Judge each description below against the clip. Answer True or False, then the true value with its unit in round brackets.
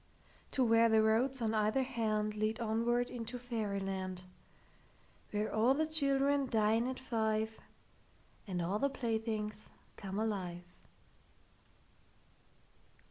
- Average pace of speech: False (100 wpm)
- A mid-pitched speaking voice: False (220 Hz)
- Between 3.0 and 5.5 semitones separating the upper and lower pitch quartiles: False (2.5 semitones)